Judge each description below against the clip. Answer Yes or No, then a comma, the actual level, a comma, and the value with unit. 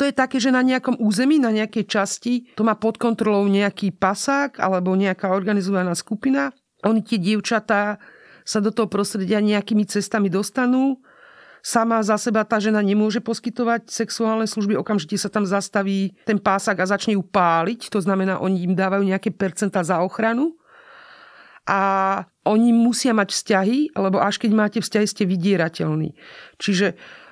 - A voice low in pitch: No, high, 210 Hz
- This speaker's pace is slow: No, average, 155 wpm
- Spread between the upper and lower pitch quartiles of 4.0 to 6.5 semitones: No, average, 2.7 semitones